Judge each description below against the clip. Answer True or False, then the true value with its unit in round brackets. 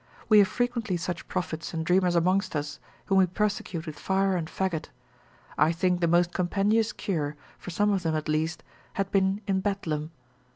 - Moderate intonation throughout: True (3.2 semitones)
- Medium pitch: True (180 Hz)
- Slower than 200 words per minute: True (180 wpm)